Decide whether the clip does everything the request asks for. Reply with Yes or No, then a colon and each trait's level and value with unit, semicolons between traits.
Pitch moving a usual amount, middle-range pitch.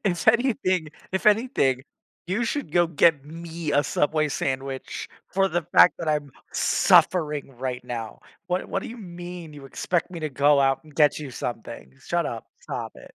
Yes: average, 4.4 semitones; medium, 160 Hz